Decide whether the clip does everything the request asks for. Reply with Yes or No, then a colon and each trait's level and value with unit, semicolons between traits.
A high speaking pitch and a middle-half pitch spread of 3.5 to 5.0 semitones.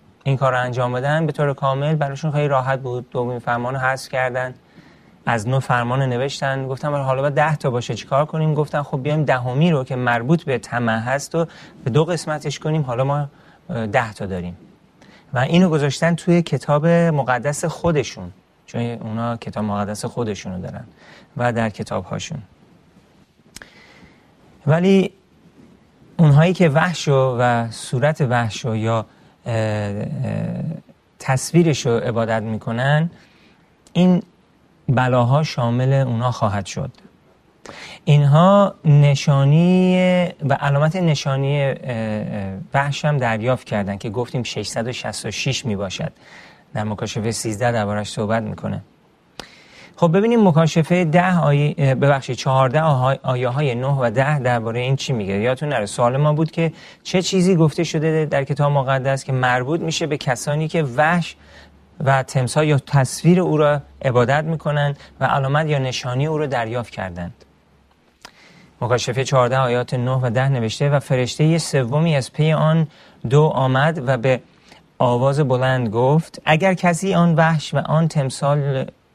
No: low, 135 Hz; average, 4.0 semitones